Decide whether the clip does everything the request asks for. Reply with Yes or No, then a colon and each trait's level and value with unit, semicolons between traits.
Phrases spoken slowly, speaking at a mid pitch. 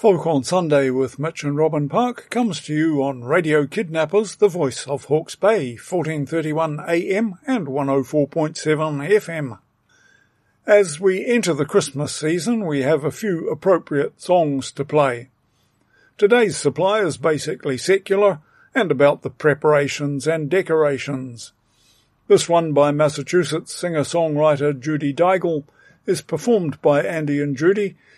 Yes: slow, 130 wpm; medium, 155 Hz